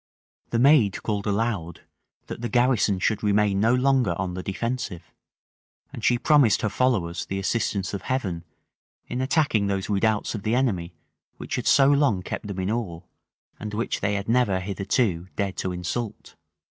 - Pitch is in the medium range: No, low, 105 Hz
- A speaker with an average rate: Yes, average, 170 wpm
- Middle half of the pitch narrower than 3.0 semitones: No, average, 4.1 semitones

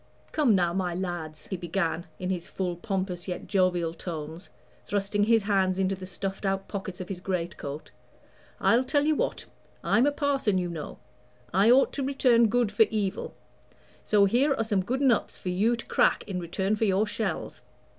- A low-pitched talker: No, high, 195 Hz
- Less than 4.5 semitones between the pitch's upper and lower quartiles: Yes, average, 3.9 semitones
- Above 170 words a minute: Yes, average, 185 wpm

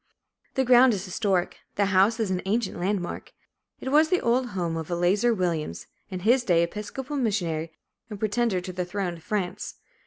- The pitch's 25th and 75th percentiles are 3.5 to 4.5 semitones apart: No, average, 4.9 semitones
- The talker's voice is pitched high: Yes, high, 200 Hz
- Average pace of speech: Yes, average, 180 wpm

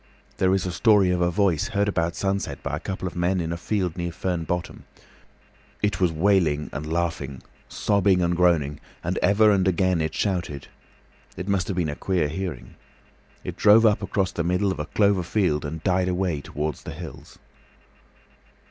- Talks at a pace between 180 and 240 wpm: Yes, average, 185 wpm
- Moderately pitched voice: No, very low, 90 Hz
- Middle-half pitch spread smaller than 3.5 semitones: Yes, average, 3.0 semitones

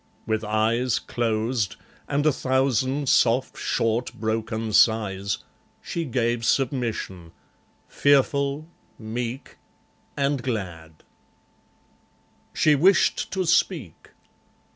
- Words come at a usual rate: No, slow, 85 wpm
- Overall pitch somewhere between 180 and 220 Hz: No, low, 120 Hz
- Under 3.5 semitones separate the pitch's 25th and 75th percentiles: No, average, 4.0 semitones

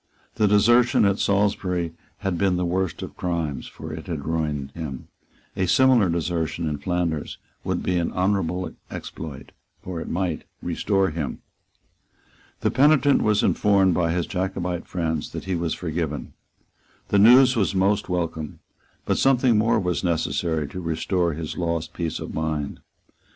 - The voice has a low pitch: Yes, very low, 90 Hz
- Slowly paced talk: No, average, 150 wpm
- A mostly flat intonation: No, average, 3.4 semitones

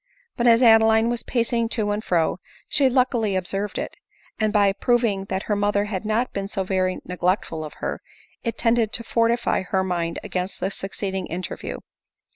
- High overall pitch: Yes, high, 205 Hz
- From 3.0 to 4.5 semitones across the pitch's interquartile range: Yes, average, 3.5 semitones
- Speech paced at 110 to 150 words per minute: No, average, 175 wpm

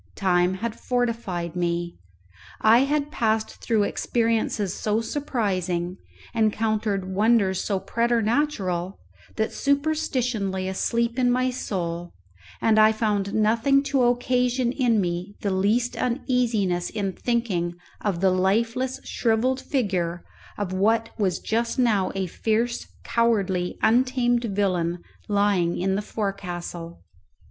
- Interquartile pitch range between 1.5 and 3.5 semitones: No, average, 4.1 semitones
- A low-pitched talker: No, high, 215 Hz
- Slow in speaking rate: Yes, slow, 120 wpm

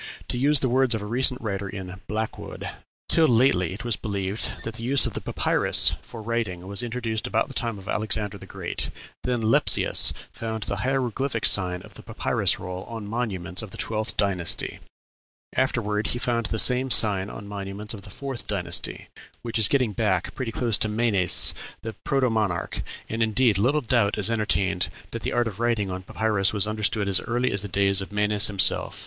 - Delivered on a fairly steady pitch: No, average, 3.2 semitones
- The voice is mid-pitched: No, low, 110 Hz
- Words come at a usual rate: Yes, average, 190 wpm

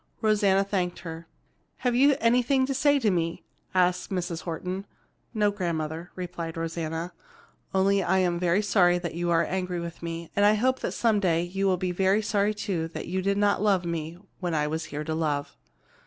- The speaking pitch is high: No, medium, 180 Hz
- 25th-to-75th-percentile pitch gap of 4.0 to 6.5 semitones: No, average, 3.3 semitones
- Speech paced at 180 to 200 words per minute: Yes, average, 190 wpm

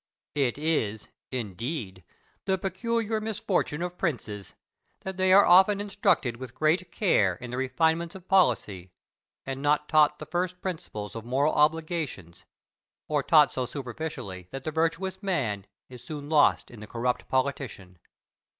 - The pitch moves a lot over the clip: Yes, wide, 6.7 semitones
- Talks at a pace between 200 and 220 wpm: No, average, 150 wpm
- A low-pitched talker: No, medium, 150 Hz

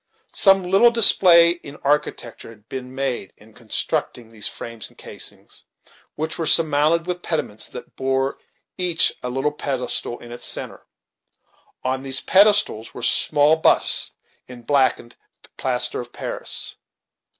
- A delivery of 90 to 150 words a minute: Yes, slow, 135 wpm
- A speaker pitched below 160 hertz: Yes, low, 135 Hz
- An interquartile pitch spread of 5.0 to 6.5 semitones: Yes, wide, 5.6 semitones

